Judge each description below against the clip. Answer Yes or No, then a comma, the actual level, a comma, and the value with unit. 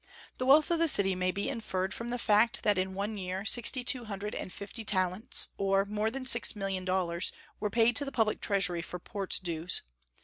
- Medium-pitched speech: No, high, 200 Hz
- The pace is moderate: No, fast, 210 wpm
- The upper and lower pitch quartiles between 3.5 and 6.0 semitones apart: Yes, average, 3.8 semitones